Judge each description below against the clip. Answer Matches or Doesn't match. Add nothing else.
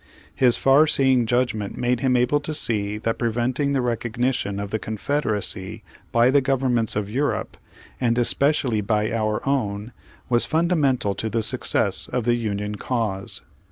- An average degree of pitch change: Matches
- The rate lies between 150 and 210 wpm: Matches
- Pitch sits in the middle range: Doesn't match